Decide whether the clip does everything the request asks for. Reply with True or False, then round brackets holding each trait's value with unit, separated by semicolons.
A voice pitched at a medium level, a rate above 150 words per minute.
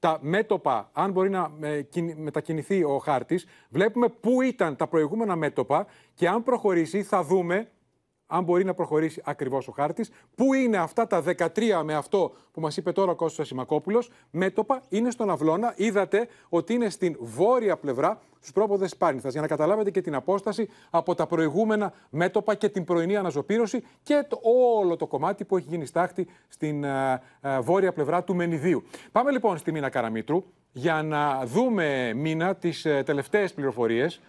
True (180 Hz; 160 wpm)